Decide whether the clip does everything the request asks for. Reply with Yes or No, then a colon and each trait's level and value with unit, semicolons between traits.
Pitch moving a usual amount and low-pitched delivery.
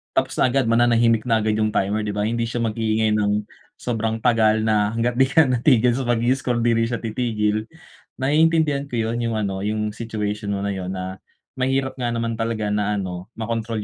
No: narrow, 2.2 semitones; low, 115 Hz